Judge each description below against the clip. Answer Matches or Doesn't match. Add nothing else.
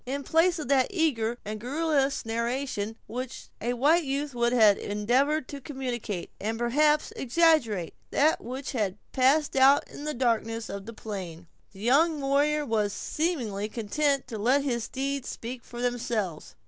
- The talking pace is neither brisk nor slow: Matches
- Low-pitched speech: Doesn't match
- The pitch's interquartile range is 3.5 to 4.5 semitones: Matches